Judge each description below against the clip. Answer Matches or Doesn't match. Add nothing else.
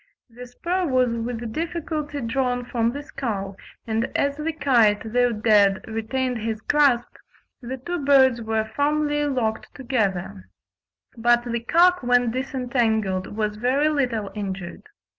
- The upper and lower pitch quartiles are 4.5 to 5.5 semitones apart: Doesn't match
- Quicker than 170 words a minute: Doesn't match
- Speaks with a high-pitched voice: Matches